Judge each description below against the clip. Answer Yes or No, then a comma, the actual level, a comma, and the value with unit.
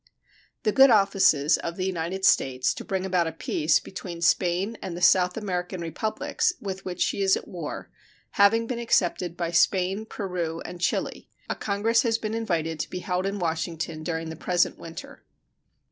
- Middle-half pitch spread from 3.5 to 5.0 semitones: No, average, 3.1 semitones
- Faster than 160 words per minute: Yes, average, 175 wpm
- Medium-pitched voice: Yes, medium, 180 Hz